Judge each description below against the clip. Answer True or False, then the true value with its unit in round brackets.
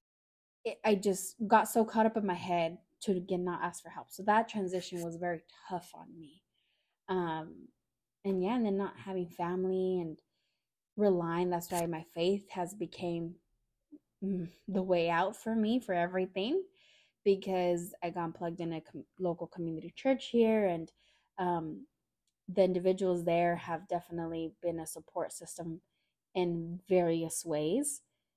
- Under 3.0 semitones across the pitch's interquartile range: True (2.4 semitones)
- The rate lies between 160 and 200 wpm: False (150 wpm)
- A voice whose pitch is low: False (180 Hz)